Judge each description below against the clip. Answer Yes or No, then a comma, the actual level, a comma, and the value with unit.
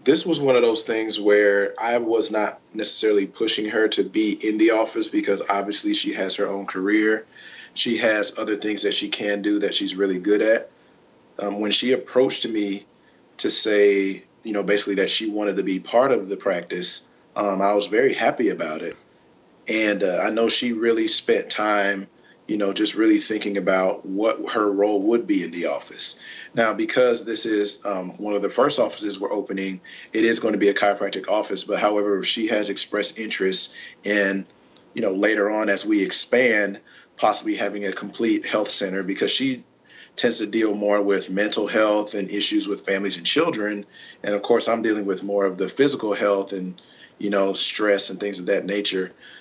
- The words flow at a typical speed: Yes, average, 195 wpm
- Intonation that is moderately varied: No, narrow, 2.2 semitones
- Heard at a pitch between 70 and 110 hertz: Yes, low, 105 Hz